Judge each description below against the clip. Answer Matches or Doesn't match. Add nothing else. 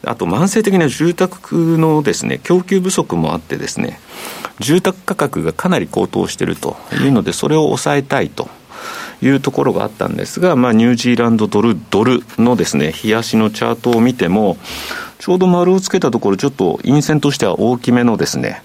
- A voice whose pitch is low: Doesn't match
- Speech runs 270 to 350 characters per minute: Doesn't match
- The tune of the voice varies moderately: Doesn't match